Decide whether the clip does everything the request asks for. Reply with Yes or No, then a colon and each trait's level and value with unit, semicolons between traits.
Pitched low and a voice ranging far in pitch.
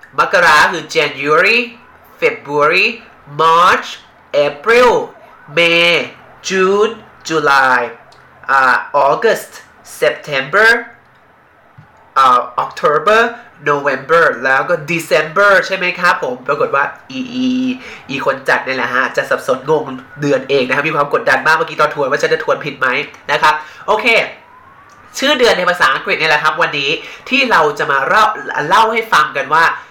No: high, 200 Hz; wide, 8.5 semitones